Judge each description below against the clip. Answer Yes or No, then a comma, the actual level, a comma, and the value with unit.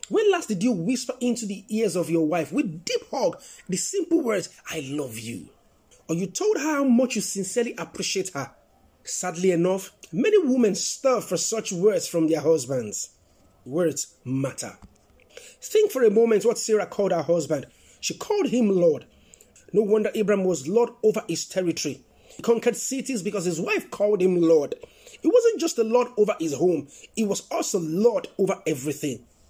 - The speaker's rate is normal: Yes, average, 175 wpm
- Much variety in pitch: Yes, wide, 6.8 semitones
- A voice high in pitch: Yes, high, 205 Hz